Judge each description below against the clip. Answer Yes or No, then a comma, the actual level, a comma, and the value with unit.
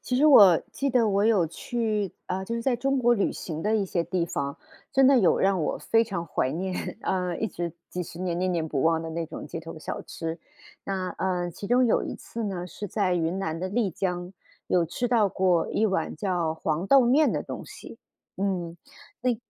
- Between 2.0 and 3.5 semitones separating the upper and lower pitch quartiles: No, average, 4.6 semitones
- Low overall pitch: No, high, 190 Hz